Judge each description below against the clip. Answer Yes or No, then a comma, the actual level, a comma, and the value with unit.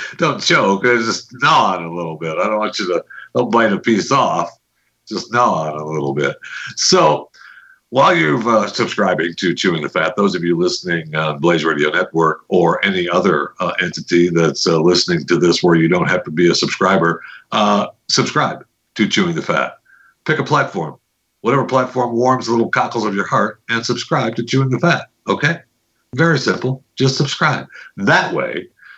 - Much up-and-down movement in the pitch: Yes, wide, 6.9 semitones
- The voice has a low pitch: Yes, low, 115 Hz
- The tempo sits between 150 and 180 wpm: No, average, 190 wpm